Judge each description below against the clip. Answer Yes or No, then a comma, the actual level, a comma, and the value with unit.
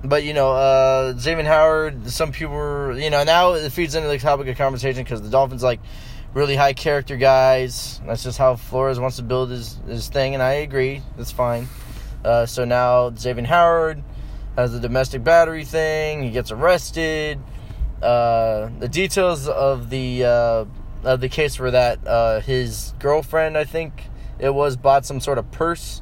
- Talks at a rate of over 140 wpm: Yes, average, 180 wpm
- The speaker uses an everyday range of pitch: Yes, average, 3.2 semitones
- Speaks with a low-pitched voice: Yes, low, 130 Hz